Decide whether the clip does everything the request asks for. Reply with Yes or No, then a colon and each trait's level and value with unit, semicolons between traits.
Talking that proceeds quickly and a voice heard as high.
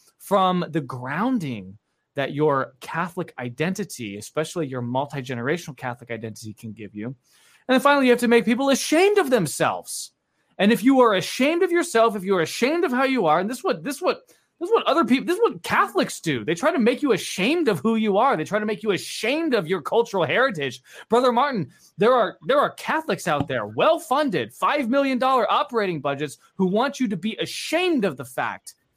Yes: fast, 215 wpm; high, 205 Hz